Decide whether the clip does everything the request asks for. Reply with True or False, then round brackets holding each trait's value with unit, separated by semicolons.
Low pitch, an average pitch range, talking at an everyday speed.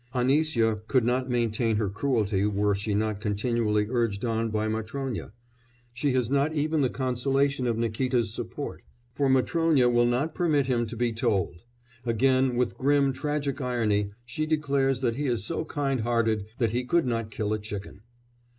True (120 Hz; 3.7 semitones; 170 wpm)